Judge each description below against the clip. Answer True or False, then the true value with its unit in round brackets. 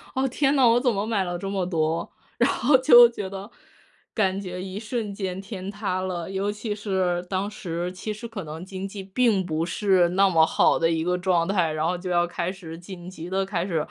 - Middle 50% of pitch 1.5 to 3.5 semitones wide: True (2.7 semitones)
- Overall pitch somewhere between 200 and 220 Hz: False (190 Hz)